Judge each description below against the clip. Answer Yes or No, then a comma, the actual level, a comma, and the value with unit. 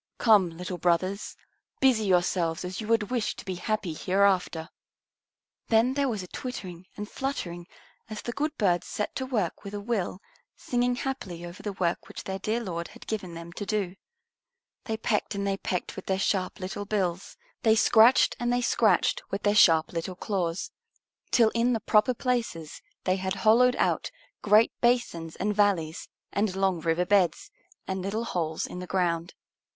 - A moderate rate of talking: Yes, average, 175 wpm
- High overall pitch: Yes, high, 195 Hz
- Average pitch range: Yes, average, 3.9 semitones